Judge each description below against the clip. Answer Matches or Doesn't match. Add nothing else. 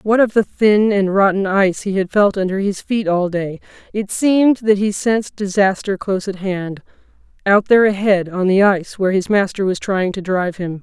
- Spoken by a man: Doesn't match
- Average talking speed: Doesn't match